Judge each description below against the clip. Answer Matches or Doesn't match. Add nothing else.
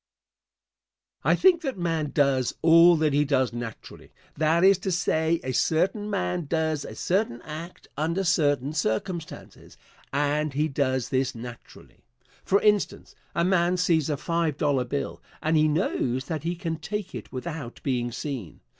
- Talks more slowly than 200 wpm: Matches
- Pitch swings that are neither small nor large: Matches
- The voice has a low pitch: Doesn't match